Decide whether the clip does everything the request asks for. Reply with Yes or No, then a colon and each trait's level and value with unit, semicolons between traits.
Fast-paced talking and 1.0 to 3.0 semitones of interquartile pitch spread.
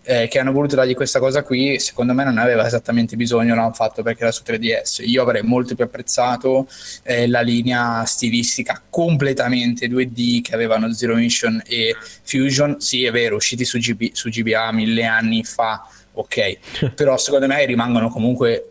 Yes: fast, 175 wpm; narrow, 2.4 semitones